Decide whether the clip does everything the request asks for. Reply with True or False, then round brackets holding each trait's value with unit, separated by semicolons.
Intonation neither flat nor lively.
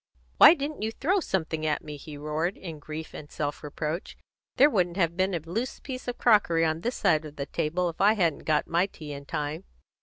True (4.9 semitones)